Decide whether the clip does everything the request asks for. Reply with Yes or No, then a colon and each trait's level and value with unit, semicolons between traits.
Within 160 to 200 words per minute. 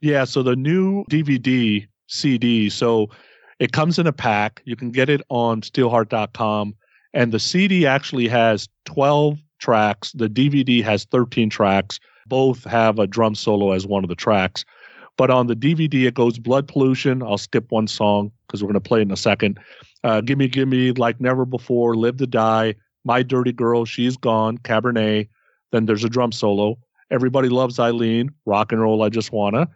Yes: average, 180 wpm